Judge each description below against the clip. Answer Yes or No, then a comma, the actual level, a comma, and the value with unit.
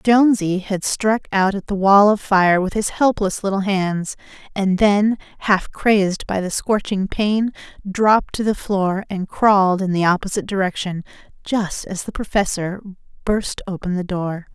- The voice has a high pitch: Yes, high, 195 Hz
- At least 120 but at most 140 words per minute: No, average, 165 wpm